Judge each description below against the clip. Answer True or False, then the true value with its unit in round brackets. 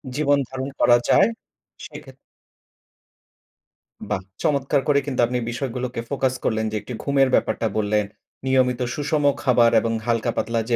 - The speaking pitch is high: False (125 Hz)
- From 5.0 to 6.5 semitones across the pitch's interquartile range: False (3.0 semitones)